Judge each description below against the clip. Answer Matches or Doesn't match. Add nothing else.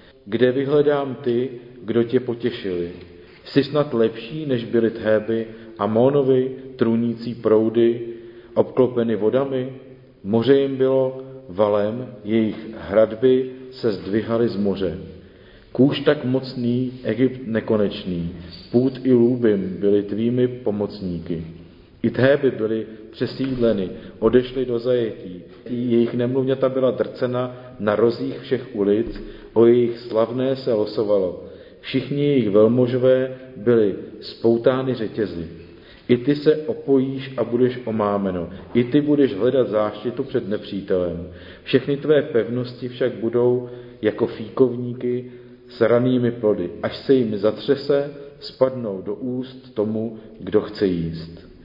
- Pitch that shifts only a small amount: Doesn't match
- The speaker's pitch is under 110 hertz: Doesn't match